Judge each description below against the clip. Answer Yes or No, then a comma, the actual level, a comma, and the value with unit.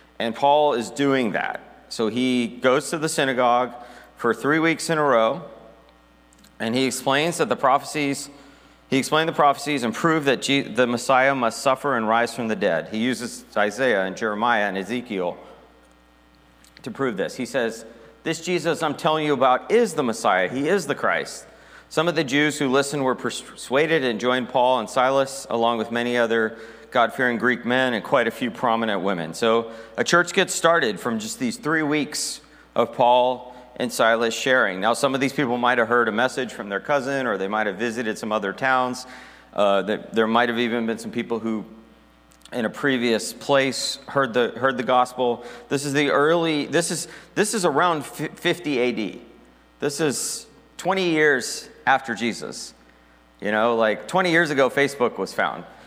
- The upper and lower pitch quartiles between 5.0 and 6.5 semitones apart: No, average, 3.9 semitones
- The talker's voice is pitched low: Yes, low, 125 Hz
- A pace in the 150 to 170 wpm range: No, average, 185 wpm